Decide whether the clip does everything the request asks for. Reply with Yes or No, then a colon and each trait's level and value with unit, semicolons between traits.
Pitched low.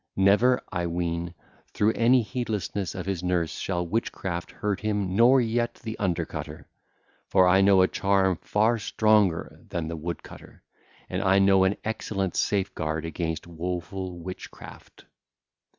Yes: very low, 95 Hz